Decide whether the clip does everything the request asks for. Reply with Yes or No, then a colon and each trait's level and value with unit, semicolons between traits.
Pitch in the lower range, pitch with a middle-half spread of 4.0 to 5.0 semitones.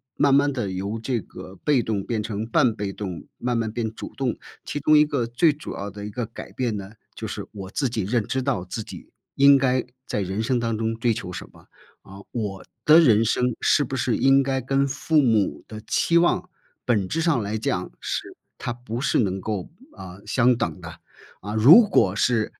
Yes: low, 115 Hz; average, 4.4 semitones